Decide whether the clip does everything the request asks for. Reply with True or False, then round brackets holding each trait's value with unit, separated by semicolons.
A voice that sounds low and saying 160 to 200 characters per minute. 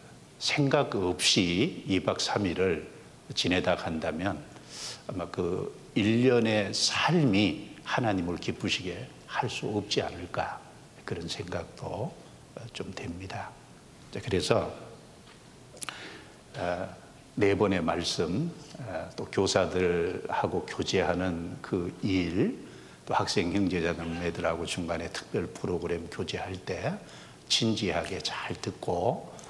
True (95 Hz; 190 characters per minute)